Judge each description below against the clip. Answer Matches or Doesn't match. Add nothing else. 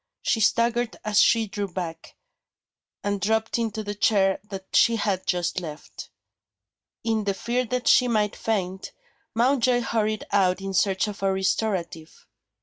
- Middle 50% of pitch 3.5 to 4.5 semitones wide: Doesn't match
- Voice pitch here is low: Doesn't match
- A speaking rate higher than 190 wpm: Doesn't match